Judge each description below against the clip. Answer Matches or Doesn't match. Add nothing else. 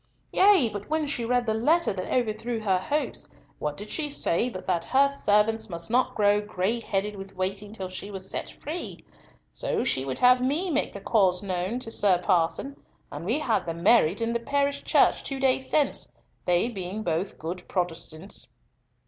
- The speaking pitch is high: Matches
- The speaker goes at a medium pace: Matches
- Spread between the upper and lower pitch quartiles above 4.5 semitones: Matches